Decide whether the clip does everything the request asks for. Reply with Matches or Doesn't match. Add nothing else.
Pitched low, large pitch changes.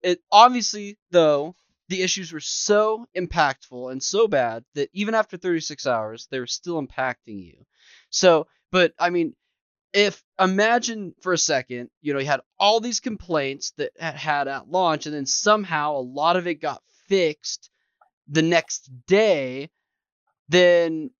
Doesn't match